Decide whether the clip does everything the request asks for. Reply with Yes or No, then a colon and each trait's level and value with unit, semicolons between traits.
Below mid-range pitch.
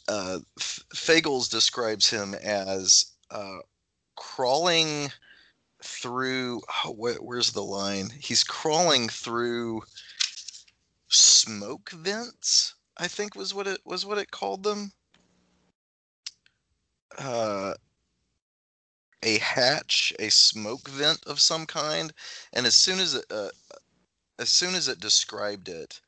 Yes: low, 120 Hz